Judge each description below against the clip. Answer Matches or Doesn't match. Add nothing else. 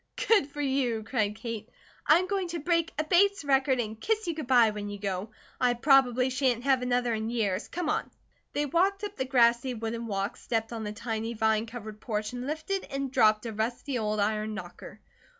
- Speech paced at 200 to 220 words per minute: Matches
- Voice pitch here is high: Matches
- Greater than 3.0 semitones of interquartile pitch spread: Matches